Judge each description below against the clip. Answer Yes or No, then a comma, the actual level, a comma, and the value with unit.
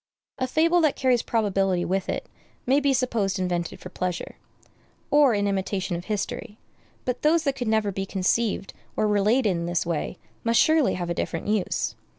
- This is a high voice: Yes, high, 210 Hz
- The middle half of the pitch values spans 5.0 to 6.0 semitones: Yes, wide, 5.4 semitones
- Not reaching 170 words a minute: No, average, 175 wpm